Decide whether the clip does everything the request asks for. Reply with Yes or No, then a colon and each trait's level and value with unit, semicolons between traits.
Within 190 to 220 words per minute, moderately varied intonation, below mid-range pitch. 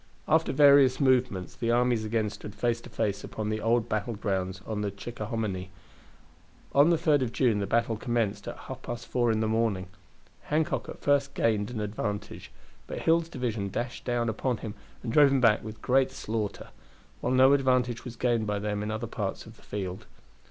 Yes: average, 195 wpm; average, 3.2 semitones; low, 115 Hz